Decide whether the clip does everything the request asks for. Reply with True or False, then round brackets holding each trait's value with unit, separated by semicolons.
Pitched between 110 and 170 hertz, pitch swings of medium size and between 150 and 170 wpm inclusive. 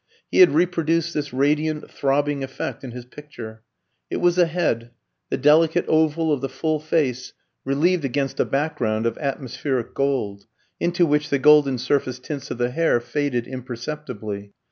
True (140 Hz; 3.7 semitones; 160 wpm)